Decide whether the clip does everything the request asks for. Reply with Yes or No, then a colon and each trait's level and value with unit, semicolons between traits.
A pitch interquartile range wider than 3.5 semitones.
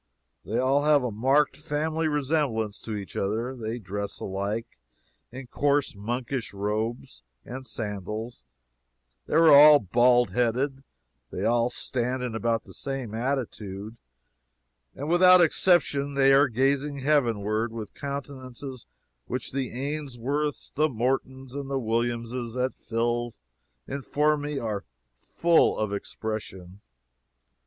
Yes: average, 4.0 semitones